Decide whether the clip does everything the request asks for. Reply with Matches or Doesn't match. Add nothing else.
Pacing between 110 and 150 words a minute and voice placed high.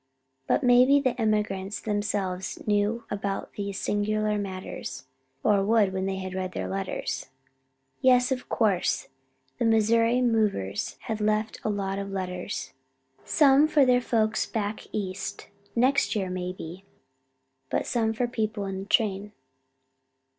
Matches